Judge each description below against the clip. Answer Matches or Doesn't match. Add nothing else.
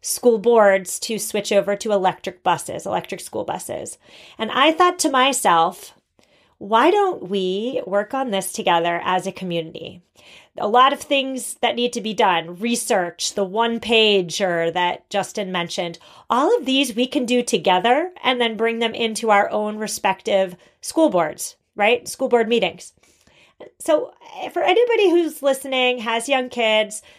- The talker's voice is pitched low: Doesn't match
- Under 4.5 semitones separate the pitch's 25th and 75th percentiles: Doesn't match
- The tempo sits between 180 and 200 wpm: Doesn't match